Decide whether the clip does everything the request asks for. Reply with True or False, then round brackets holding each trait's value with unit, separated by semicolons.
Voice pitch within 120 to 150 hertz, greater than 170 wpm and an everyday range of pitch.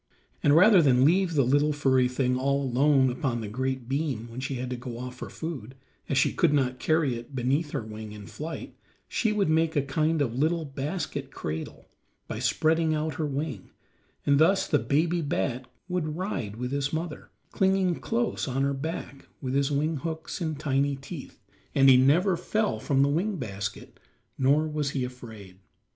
True (140 Hz; 185 wpm; 3.7 semitones)